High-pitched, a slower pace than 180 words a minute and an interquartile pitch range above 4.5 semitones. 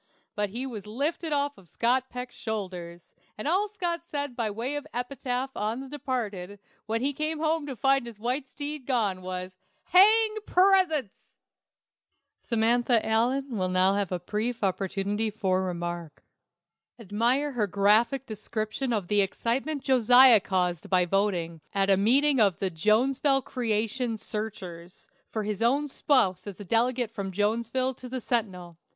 Yes: high, 230 Hz; average, 150 wpm; average, 5.2 semitones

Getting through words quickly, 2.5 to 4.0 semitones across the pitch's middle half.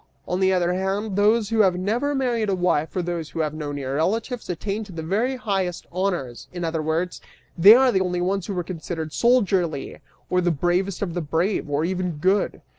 Yes: fast, 210 wpm; average, 3.5 semitones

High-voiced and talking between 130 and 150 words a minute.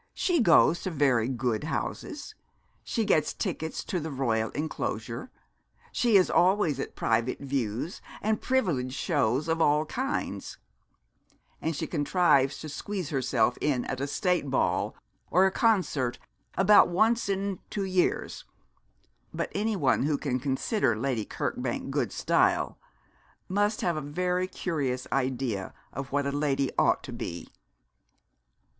No: medium, 150 Hz; average, 140 wpm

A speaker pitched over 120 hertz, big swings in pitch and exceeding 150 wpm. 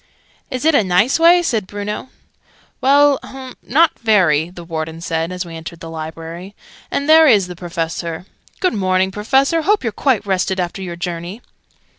Yes: high, 190 Hz; wide, 7.5 semitones; average, 170 wpm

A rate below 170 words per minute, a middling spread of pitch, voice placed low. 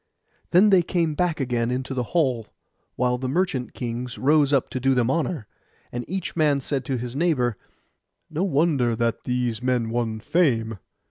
No: average, 175 wpm; average, 4.4 semitones; low, 130 Hz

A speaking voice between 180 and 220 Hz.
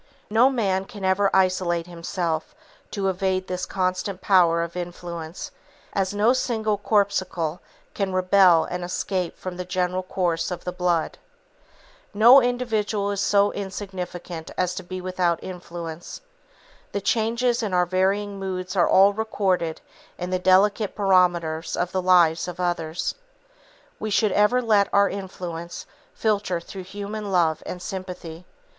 Yes: medium, 185 Hz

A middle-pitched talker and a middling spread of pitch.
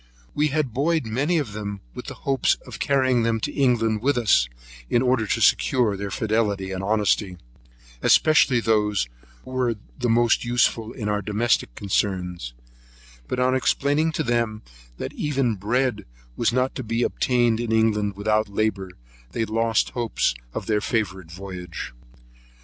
No: low, 115 Hz; average, 3.4 semitones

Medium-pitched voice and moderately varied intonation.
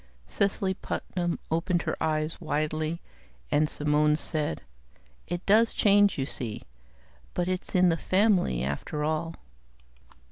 Yes: medium, 165 Hz; average, 3.4 semitones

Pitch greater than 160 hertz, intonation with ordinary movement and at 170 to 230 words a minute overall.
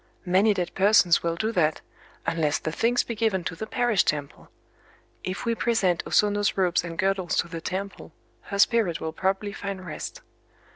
Yes: high, 190 Hz; average, 3.7 semitones; average, 175 wpm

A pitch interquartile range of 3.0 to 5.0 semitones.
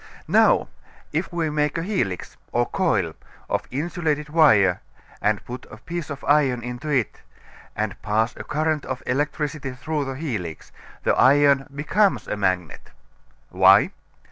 Yes: average, 4.3 semitones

